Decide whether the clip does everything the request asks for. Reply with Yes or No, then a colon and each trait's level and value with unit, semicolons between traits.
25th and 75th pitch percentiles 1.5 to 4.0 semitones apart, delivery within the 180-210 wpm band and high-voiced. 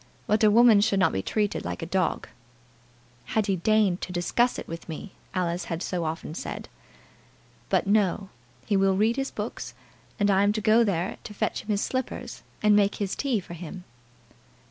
Yes: average, 3.1 semitones; average, 190 wpm; high, 200 Hz